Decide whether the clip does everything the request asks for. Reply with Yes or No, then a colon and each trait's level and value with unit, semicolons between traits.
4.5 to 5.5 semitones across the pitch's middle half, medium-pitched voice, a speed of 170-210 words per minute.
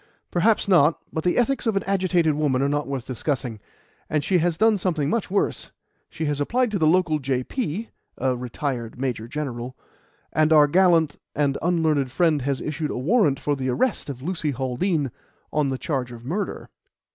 Yes: average, 5.1 semitones; medium, 150 Hz; average, 180 wpm